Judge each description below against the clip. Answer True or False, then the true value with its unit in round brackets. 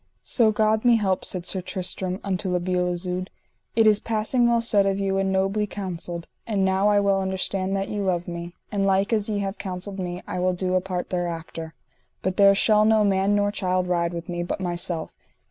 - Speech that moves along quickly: True (215 wpm)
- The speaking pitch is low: False (190 Hz)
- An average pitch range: False (2.2 semitones)